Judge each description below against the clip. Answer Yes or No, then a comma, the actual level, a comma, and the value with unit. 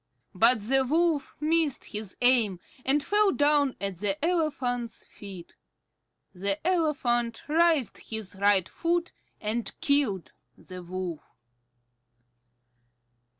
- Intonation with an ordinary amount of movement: No, wide, 7.0 semitones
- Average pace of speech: No, slow, 105 wpm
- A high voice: Yes, high, 245 Hz